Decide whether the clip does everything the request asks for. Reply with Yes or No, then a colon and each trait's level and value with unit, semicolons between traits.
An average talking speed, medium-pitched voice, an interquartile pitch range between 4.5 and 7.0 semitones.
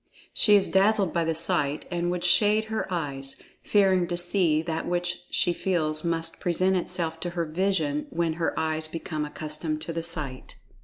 No: average, 175 wpm; medium, 170 Hz; narrow, 2.4 semitones